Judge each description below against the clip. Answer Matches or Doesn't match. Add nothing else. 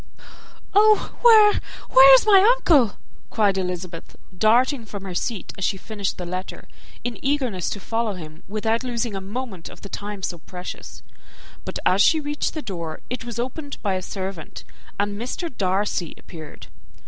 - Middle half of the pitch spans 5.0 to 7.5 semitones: Matches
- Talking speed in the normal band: Matches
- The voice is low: Doesn't match